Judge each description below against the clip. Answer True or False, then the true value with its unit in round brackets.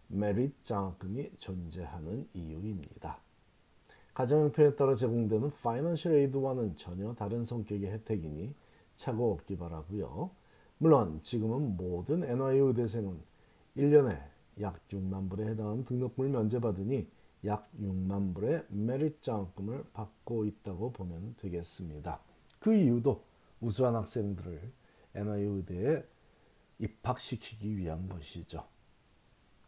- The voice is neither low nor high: False (105 Hz)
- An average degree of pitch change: True (4.8 semitones)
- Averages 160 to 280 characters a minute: True (275 characters per minute)